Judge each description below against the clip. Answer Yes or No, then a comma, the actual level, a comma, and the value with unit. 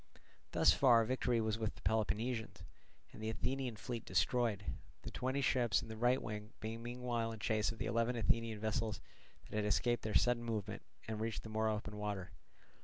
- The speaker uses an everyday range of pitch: No, narrow, 1.9 semitones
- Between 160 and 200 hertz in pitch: No, low, 110 Hz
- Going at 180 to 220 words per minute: Yes, average, 185 wpm